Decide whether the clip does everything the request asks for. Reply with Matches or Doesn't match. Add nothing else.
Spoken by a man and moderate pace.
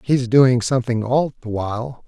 Matches